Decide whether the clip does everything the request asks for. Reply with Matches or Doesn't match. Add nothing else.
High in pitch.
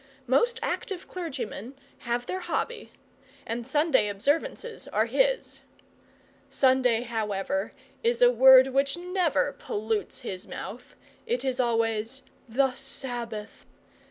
Matches